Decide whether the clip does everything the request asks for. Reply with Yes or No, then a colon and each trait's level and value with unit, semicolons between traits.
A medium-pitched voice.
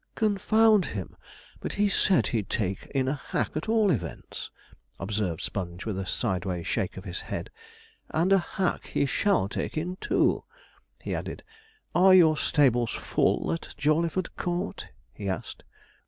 Yes: medium, 150 Hz